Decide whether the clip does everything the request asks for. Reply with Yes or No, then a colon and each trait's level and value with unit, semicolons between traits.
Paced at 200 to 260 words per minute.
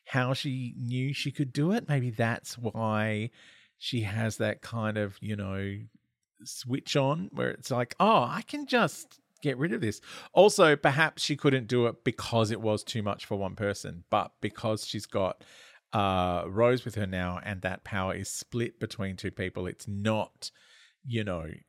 No: average, 180 wpm